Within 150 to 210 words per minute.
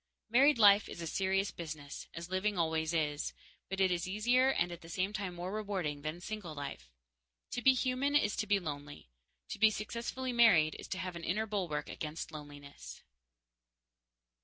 Yes: average, 175 wpm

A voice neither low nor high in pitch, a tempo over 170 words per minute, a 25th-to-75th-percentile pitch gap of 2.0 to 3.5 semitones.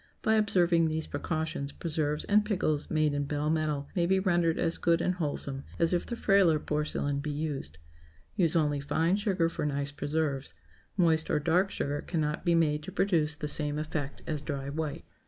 Yes: medium, 155 Hz; average, 185 wpm; narrow, 2.6 semitones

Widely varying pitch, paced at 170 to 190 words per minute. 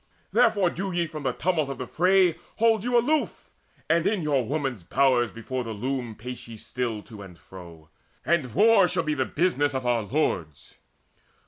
Yes: wide, 7.0 semitones; average, 180 wpm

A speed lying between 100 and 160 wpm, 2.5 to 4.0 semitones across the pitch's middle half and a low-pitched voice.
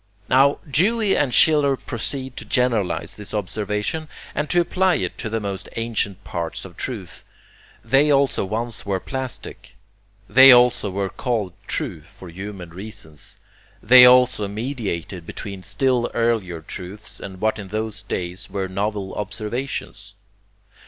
No: average, 140 wpm; average, 4.9 semitones; low, 110 Hz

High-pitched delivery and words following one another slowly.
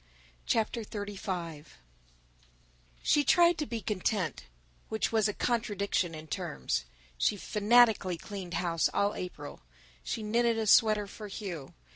Yes: high, 205 Hz; slow, 125 wpm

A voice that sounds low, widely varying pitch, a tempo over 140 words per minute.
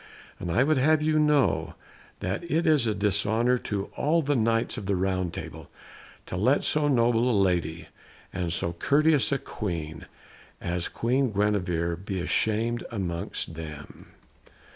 Yes: low, 110 Hz; wide, 6.9 semitones; average, 150 wpm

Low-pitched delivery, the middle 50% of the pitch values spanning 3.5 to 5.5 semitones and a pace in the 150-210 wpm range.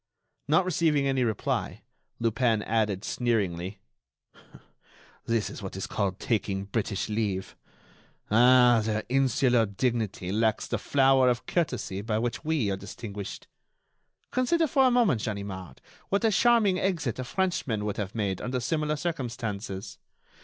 No: low, 115 Hz; average, 5.2 semitones; slow, 135 wpm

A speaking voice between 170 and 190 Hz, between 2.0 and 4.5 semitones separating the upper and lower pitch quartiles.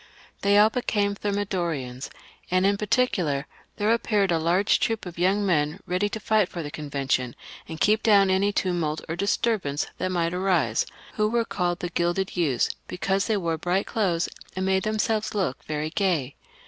Yes: medium, 185 Hz; average, 3.8 semitones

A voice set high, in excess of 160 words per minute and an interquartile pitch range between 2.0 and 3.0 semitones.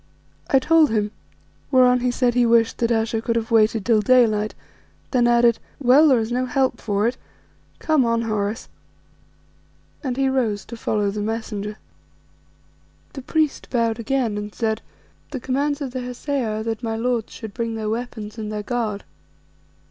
Yes: high, 230 Hz; average, 170 wpm; narrow, 2.6 semitones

